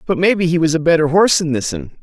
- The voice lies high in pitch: No, medium, 160 Hz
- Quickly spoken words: Yes, fast, 265 wpm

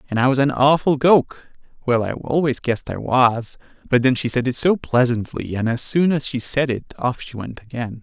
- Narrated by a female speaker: No, male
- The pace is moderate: No, fast, 225 wpm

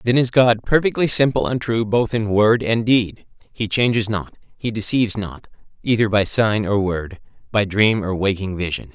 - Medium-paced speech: Yes, average, 190 wpm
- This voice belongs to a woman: No, male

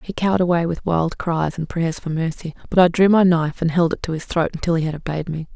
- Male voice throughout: No, female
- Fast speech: Yes, fast, 280 wpm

